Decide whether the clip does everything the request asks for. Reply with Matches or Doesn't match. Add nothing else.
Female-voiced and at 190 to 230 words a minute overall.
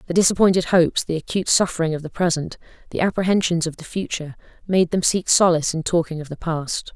Matches